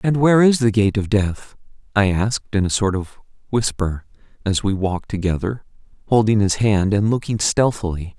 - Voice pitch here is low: Yes, low, 105 Hz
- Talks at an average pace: Yes, average, 175 wpm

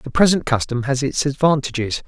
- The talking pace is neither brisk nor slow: Yes, average, 175 wpm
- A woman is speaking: No, male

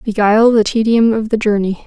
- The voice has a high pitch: Yes, high, 215 Hz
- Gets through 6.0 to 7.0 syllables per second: No, 5.7 syllables/s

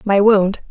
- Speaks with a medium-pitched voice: No, high, 200 Hz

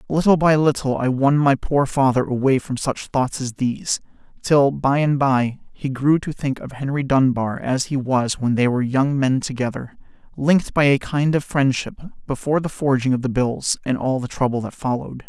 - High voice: No, low, 135 Hz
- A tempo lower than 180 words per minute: No, fast, 205 wpm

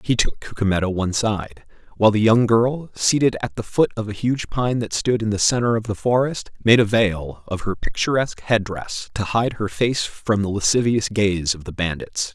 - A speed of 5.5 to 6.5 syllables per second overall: No, 5.0 syllables/s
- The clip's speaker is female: No, male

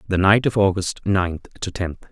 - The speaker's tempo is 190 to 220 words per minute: Yes, average, 200 wpm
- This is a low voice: Yes, very low, 95 Hz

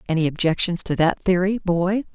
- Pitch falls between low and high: Yes, medium, 180 Hz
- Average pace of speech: Yes, average, 170 wpm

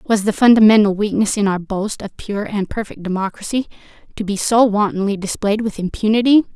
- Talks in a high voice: Yes, high, 210 Hz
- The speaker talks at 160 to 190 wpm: Yes, average, 175 wpm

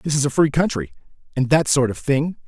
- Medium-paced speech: No, fast, 240 wpm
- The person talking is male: Yes, male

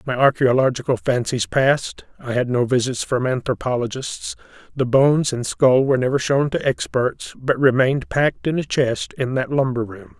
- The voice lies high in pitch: No, low, 130 Hz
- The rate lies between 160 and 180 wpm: Yes, average, 170 wpm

